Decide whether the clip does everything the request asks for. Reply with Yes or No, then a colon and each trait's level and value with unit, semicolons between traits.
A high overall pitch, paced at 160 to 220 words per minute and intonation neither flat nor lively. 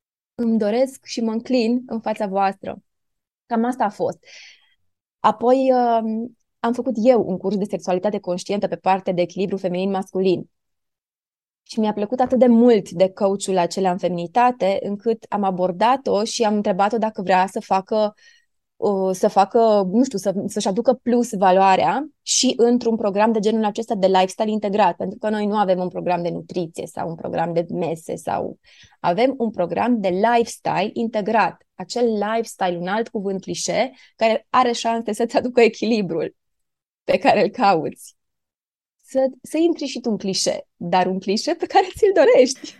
Yes: high, 215 Hz; average, 165 wpm; average, 3.9 semitones